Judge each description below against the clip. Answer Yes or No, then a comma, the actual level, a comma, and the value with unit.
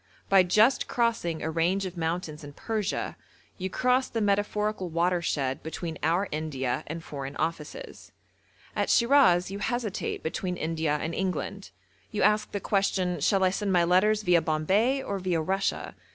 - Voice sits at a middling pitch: Yes, medium, 180 Hz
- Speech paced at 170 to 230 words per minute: No, average, 155 wpm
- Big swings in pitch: No, average, 4.1 semitones